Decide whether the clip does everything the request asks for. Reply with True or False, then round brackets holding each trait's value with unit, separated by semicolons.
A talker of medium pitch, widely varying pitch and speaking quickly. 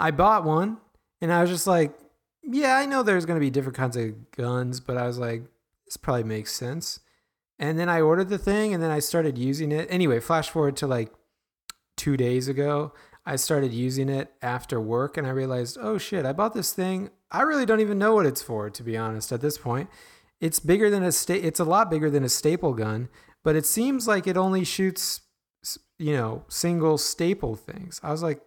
True (155 Hz; 6.2 semitones; 215 wpm)